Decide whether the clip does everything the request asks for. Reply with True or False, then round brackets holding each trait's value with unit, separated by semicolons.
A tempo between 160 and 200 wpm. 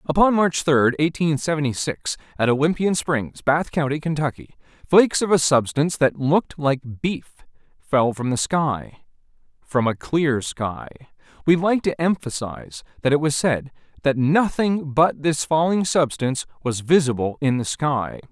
False (150 wpm)